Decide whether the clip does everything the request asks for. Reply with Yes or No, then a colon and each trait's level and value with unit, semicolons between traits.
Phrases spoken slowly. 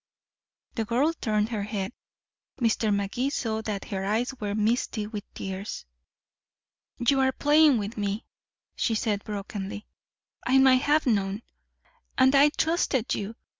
Yes: slow, 130 wpm